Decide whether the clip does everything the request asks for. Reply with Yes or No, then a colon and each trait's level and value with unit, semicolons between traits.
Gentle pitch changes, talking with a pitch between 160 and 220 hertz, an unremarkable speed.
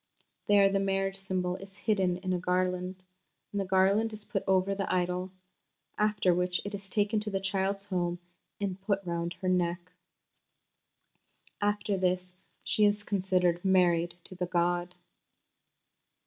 Yes: narrow, 1.7 semitones; high, 190 Hz; average, 150 wpm